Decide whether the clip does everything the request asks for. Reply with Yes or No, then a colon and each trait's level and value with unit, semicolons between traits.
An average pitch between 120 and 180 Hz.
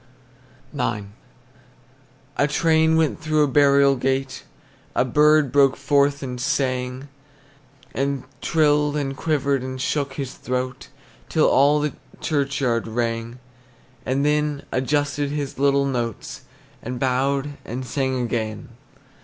Yes: medium, 140 Hz